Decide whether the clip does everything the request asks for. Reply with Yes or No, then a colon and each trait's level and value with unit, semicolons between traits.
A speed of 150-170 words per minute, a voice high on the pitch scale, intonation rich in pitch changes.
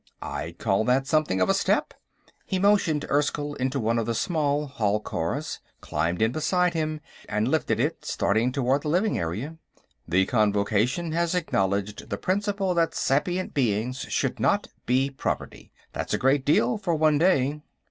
No: average, 165 wpm; medium, 140 Hz; wide, 6.4 semitones